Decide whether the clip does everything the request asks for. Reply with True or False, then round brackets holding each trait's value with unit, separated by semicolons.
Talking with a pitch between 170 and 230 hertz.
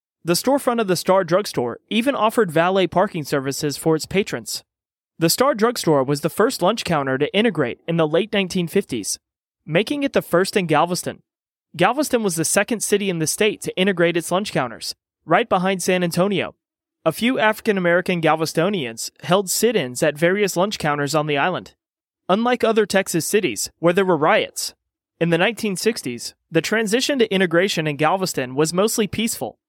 True (185 Hz)